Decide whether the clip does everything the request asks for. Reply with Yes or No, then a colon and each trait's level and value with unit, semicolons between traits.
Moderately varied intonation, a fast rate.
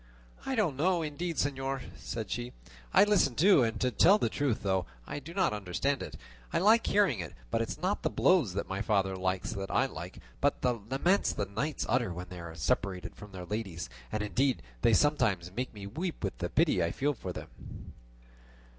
No: wide, 8.0 semitones; fast, 210 wpm